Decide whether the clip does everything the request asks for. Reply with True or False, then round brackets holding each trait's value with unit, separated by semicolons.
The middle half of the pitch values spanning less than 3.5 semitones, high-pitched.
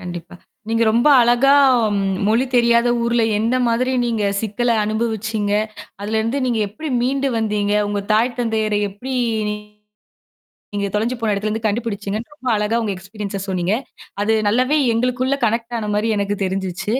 True (2.5 semitones; 220 Hz)